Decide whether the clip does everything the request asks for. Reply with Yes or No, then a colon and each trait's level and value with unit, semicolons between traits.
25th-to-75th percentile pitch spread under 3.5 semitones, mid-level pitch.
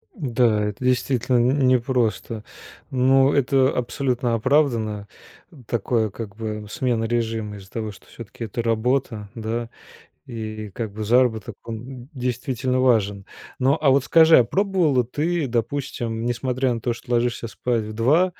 No: average, 2.7 semitones; low, 120 Hz